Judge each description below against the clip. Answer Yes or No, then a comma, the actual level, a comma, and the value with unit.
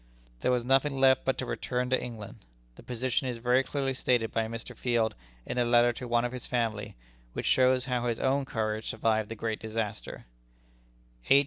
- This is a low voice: Yes, low, 120 Hz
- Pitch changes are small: Yes, narrow, 2.3 semitones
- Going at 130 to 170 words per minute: No, average, 195 wpm